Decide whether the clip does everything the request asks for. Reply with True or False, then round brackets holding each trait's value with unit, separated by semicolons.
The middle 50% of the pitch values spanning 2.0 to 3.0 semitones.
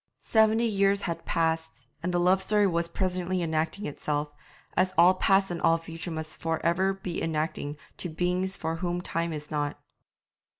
True (2.6 semitones)